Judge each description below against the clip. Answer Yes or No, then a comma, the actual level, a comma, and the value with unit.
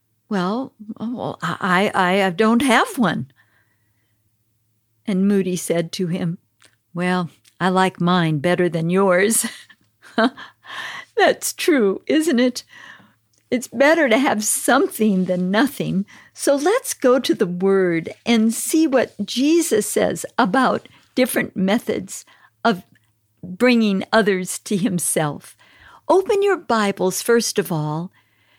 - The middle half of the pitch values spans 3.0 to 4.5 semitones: No, wide, 5.6 semitones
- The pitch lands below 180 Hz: No, high, 195 Hz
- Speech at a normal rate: No, slow, 120 wpm